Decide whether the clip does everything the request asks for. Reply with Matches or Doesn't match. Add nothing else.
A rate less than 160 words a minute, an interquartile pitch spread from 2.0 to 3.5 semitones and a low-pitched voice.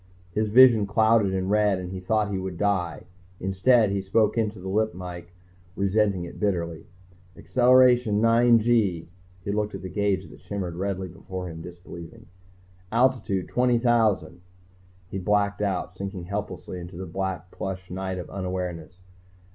Matches